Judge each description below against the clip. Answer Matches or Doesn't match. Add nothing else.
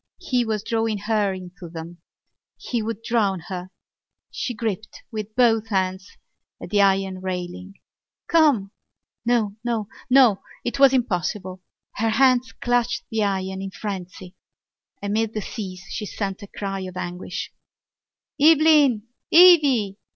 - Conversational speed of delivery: Doesn't match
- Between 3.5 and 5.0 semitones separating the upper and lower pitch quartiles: Matches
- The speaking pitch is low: Doesn't match